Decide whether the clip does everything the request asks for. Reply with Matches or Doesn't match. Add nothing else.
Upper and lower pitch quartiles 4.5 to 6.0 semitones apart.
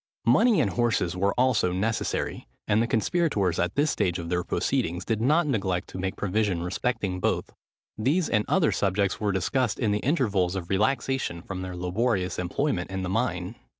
Matches